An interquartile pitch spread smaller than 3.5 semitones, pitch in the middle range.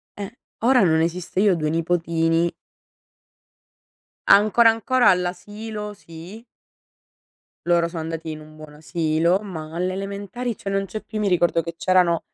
No: average, 3.9 semitones; medium, 180 Hz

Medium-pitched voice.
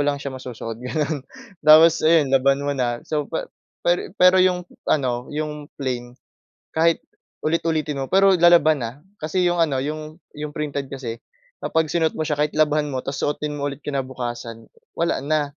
Yes: medium, 150 Hz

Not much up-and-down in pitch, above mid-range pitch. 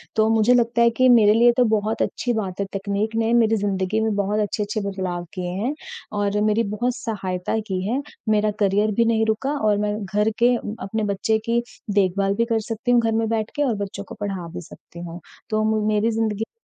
Yes: narrow, 2.2 semitones; high, 215 Hz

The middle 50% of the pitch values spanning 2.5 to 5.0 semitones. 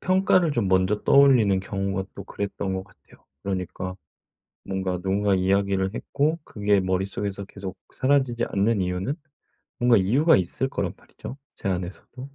Yes: average, 4.1 semitones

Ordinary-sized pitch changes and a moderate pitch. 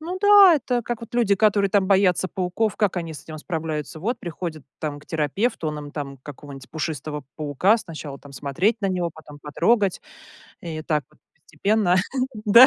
No: wide, 5.8 semitones; medium, 175 Hz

